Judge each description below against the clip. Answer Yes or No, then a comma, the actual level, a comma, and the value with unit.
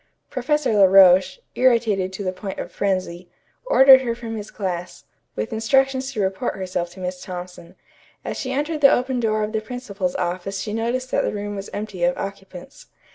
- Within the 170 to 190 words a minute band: Yes, average, 185 wpm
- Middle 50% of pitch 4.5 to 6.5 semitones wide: Yes, average, 5.0 semitones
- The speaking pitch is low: No, high, 205 Hz